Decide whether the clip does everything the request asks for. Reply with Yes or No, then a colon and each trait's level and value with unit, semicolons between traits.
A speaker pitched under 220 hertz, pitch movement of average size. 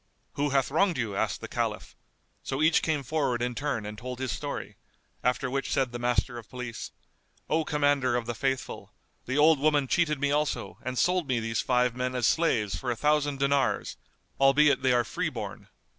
Yes: low, 135 Hz; average, 3.1 semitones